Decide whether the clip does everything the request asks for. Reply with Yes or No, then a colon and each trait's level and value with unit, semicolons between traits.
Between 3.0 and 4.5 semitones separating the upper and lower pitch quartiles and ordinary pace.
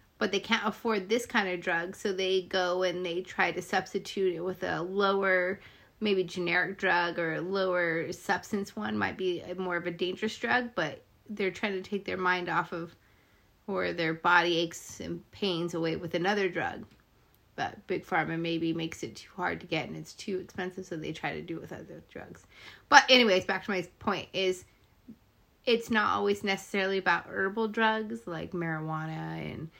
No: narrow, 2.6 semitones; average, 190 wpm